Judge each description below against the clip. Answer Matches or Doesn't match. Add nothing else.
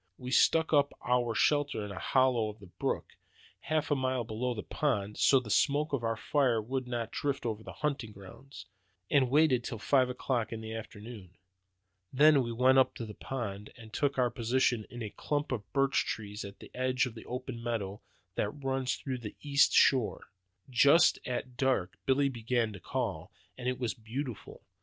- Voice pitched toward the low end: Matches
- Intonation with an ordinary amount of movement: Matches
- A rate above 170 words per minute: Matches